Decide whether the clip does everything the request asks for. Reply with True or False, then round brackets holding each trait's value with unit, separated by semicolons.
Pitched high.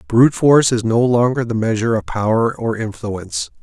False (115 Hz)